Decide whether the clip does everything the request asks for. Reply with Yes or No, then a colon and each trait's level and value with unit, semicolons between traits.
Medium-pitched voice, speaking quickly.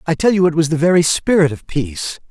Yes: medium, 160 Hz; fast, 260 wpm